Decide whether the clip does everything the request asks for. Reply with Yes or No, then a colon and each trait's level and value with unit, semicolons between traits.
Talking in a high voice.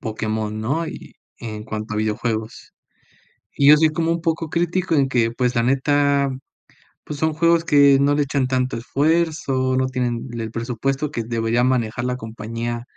No: low, 130 Hz